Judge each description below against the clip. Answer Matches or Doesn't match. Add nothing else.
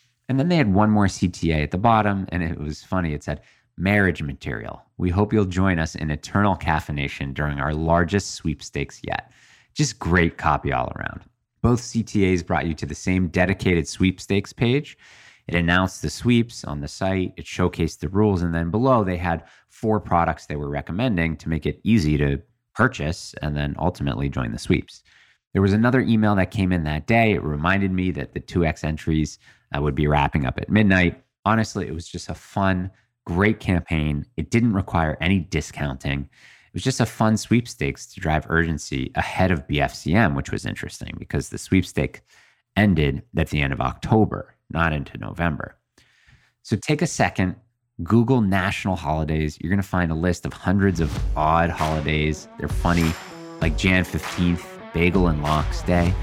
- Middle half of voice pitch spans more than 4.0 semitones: Matches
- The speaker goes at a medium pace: Matches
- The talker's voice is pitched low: Matches